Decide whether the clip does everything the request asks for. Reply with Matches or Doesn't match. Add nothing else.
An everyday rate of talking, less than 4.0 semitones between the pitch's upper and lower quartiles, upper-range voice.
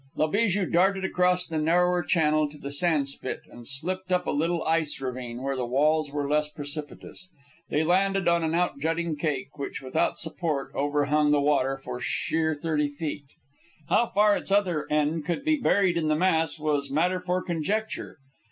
Doesn't match